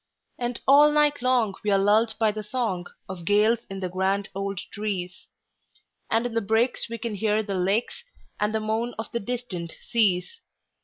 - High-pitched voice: Yes, high, 215 Hz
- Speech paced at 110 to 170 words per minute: Yes, average, 165 wpm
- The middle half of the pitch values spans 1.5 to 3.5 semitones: Yes, average, 3.2 semitones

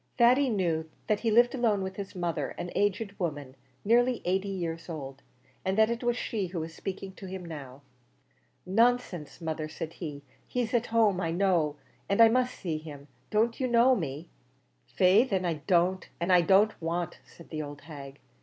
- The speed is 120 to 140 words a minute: No, average, 185 wpm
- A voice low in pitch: No, medium, 185 Hz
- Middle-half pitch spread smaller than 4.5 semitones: No, wide, 5.4 semitones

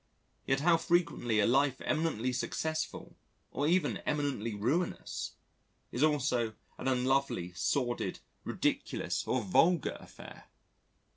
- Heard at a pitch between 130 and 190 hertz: Yes, low, 135 Hz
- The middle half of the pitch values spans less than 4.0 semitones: No, average, 4.4 semitones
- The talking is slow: Yes, slow, 110 wpm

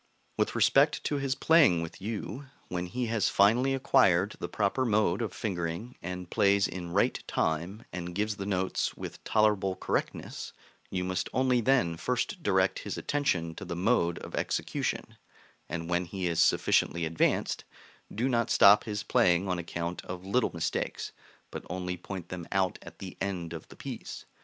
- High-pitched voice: No, very low, 95 Hz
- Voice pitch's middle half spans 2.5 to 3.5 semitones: No, average, 4.1 semitones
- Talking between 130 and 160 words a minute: No, average, 170 wpm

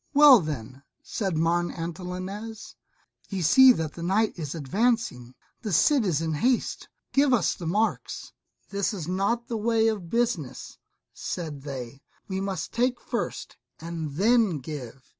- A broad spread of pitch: Yes, wide, 6.2 semitones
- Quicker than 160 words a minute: No, average, 145 wpm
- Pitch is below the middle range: No, medium, 185 Hz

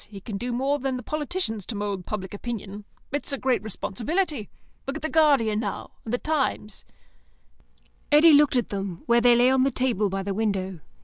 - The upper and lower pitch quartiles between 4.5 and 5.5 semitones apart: Yes, average, 5.2 semitones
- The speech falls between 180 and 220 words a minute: Yes, average, 195 wpm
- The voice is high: Yes, high, 235 Hz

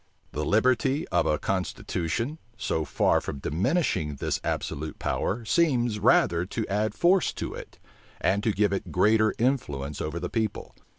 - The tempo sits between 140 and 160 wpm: Yes, average, 155 wpm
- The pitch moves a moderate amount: No, wide, 6.4 semitones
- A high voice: No, low, 105 Hz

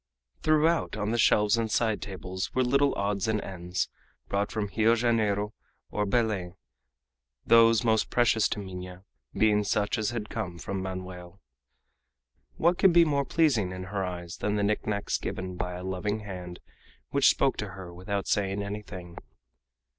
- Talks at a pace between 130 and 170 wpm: Yes, average, 160 wpm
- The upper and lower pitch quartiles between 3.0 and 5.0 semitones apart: Yes, average, 3.5 semitones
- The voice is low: Yes, low, 105 Hz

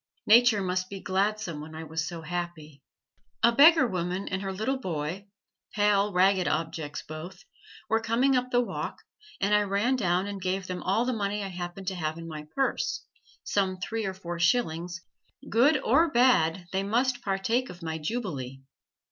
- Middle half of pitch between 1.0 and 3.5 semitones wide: No, average, 4.6 semitones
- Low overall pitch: No, high, 190 Hz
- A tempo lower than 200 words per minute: Yes, average, 175 wpm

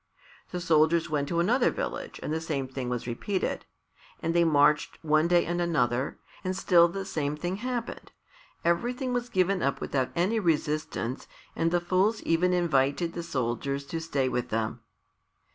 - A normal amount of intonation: Yes, average, 4.3 semitones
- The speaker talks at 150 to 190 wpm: Yes, average, 165 wpm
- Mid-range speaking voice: Yes, medium, 165 Hz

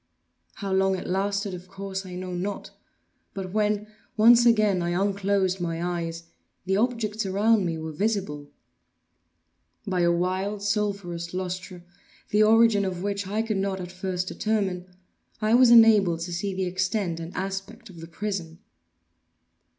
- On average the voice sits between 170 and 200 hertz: Yes, high, 190 Hz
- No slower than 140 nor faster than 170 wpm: Yes, average, 150 wpm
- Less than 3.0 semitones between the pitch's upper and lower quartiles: Yes, narrow, 2.6 semitones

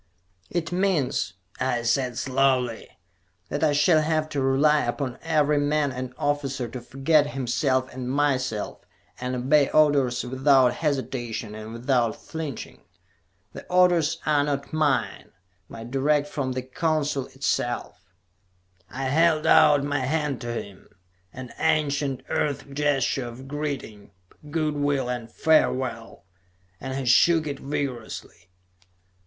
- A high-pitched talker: No, low, 135 Hz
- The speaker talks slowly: Yes, slow, 125 wpm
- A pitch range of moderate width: Yes, average, 3.0 semitones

